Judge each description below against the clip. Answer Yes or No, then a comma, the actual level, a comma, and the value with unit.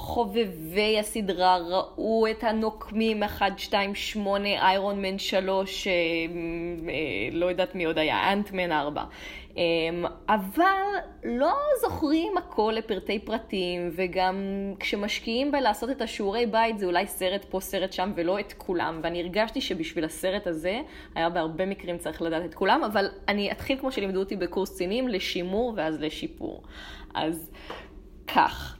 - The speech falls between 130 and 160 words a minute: Yes, average, 140 wpm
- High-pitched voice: Yes, high, 195 Hz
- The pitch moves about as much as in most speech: Yes, average, 3.8 semitones